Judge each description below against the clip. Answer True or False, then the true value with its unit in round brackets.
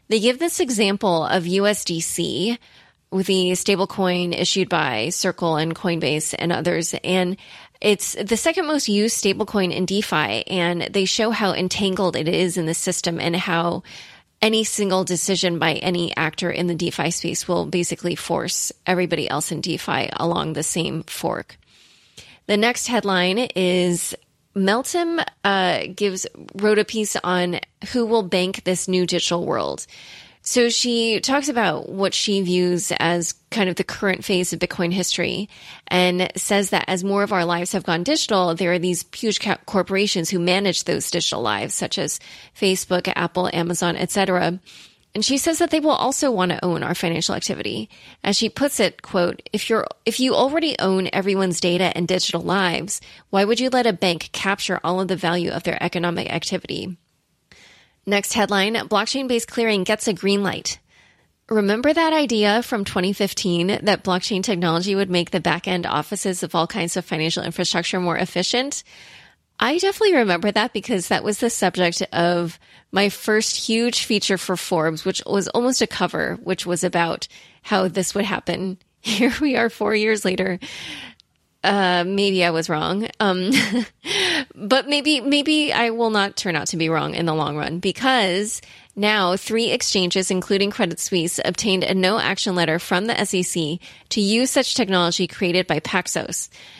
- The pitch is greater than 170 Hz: True (190 Hz)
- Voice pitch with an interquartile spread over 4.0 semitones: False (3.5 semitones)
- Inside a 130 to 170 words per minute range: True (165 wpm)